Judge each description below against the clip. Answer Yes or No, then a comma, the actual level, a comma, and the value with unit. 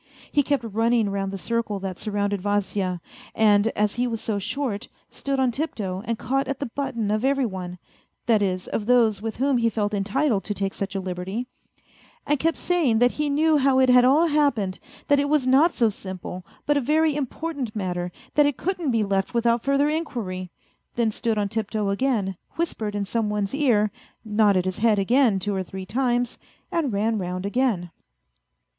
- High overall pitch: Yes, high, 225 Hz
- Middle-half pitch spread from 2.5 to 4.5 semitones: No, average, 5.2 semitones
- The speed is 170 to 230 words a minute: Yes, average, 190 wpm